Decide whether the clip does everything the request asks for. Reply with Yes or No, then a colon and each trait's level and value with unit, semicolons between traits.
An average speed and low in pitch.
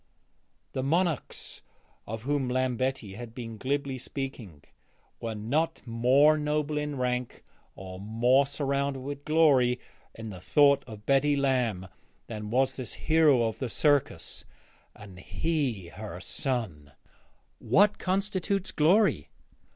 No: slow, 120 wpm; low, 130 Hz